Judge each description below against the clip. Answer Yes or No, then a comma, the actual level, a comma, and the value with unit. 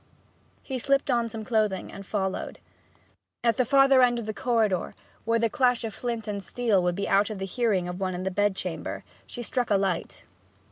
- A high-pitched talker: Yes, high, 215 Hz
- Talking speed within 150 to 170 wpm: No, fast, 205 wpm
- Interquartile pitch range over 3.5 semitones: Yes, average, 3.9 semitones